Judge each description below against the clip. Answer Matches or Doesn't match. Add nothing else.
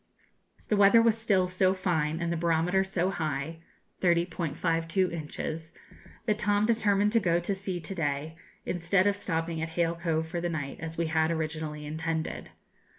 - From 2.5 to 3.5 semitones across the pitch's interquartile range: Matches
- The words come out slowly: Doesn't match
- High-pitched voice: Doesn't match